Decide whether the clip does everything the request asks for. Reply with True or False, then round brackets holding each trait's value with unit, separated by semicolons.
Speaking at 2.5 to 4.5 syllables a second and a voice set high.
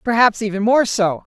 False (5.1 syllables/s; 215 Hz)